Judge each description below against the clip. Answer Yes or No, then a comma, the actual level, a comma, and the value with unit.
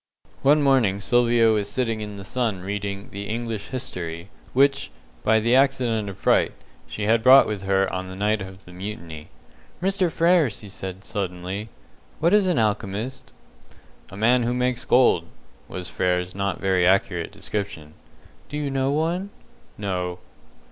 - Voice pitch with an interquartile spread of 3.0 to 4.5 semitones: No, average, 4.9 semitones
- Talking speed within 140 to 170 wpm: Yes, average, 155 wpm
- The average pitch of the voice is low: Yes, low, 105 Hz